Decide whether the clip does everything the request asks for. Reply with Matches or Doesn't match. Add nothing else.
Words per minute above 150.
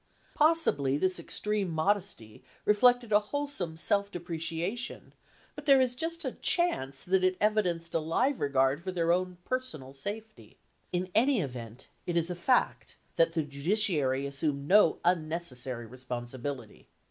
Doesn't match